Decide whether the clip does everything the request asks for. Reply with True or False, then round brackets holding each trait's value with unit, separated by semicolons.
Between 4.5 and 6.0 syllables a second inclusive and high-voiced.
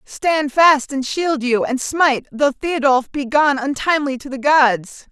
False (4.0 syllables/s; 275 Hz)